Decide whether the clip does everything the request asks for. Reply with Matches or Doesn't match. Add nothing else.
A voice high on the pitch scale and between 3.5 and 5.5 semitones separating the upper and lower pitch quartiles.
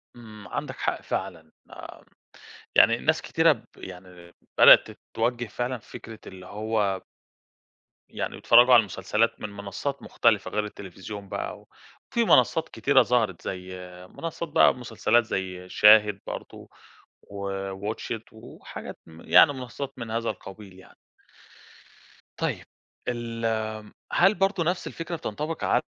Doesn't match